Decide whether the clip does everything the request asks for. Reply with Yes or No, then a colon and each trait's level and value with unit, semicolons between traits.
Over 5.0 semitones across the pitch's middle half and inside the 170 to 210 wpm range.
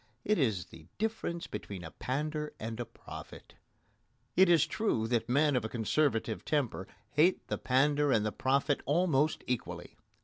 No: wide, 5.4 semitones; average, 160 wpm